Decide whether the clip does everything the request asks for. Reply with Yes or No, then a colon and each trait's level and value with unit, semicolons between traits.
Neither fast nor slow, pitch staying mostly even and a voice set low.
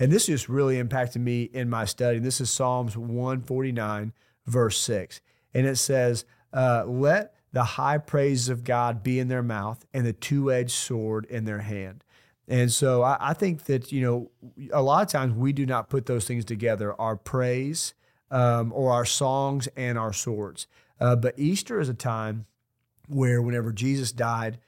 Yes: average, 180 wpm; narrow, 2.2 semitones; low, 125 Hz